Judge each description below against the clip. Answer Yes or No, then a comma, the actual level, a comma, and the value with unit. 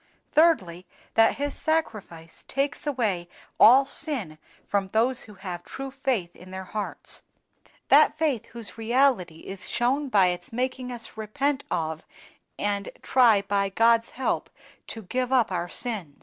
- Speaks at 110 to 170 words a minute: Yes, average, 145 wpm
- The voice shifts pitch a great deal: Yes, wide, 5.7 semitones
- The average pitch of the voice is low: No, high, 225 Hz